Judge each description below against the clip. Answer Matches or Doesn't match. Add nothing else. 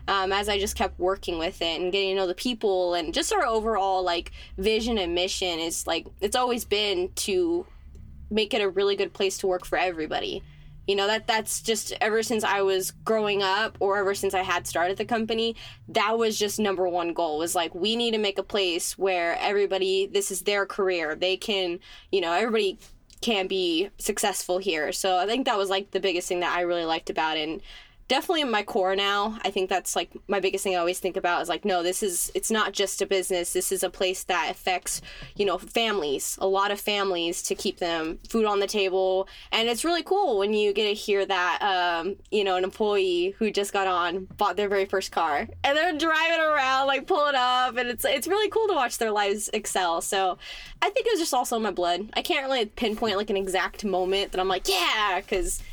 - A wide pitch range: Doesn't match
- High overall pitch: Matches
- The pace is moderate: Doesn't match